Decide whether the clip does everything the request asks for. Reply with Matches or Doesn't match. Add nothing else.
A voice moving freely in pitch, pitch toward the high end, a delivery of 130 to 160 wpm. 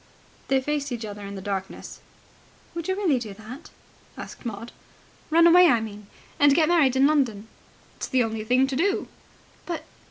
Doesn't match